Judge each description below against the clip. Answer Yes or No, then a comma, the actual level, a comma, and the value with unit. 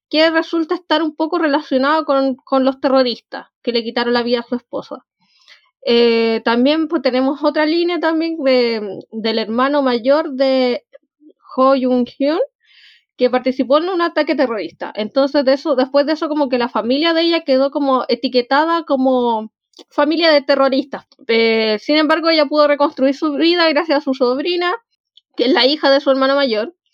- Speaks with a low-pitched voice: No, very high, 275 Hz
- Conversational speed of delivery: Yes, average, 175 wpm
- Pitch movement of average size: Yes, average, 3.6 semitones